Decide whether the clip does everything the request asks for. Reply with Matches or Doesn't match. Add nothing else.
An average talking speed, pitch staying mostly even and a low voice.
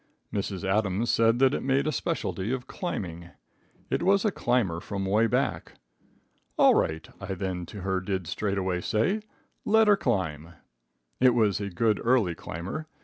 Doesn't match